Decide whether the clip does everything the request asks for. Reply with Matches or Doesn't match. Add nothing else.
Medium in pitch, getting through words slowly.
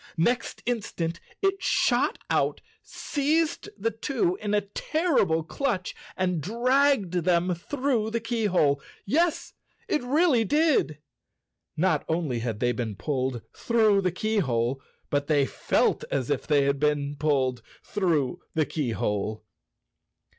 Matches